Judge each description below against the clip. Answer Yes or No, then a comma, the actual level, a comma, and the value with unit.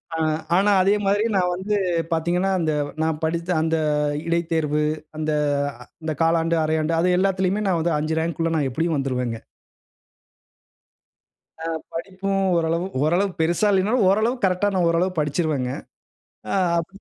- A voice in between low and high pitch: Yes, medium, 170 Hz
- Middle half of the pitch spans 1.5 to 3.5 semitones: Yes, average, 3.0 semitones